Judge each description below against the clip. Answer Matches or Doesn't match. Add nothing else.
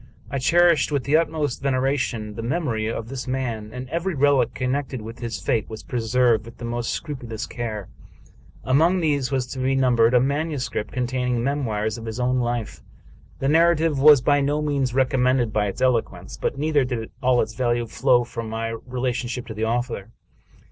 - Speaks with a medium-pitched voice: Doesn't match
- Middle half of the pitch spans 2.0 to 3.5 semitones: Matches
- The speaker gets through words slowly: Doesn't match